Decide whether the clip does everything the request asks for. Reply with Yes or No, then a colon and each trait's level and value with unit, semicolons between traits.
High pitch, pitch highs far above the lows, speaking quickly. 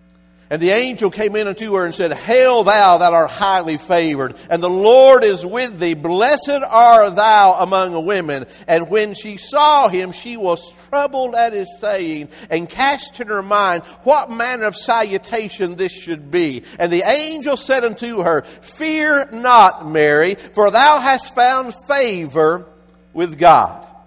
No: high, 205 Hz; wide, 6.1 semitones; average, 160 wpm